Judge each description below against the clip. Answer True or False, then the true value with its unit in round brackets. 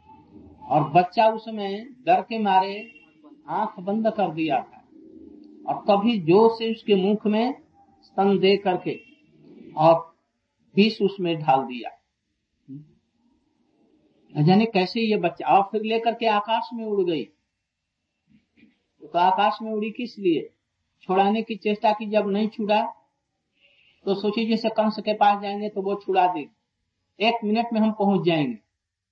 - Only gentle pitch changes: False (3.5 semitones)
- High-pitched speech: True (210 Hz)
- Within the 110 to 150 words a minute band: True (140 wpm)